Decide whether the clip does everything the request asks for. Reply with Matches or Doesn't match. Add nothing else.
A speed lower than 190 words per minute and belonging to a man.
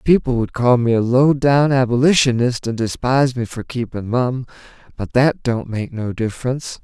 Matches